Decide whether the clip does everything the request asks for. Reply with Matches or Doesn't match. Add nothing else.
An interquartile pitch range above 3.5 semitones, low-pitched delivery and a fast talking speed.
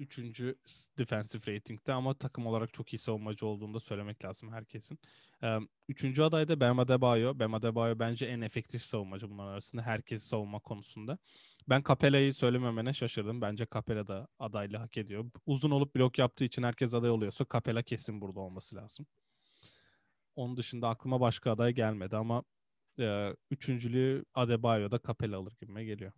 Doesn't match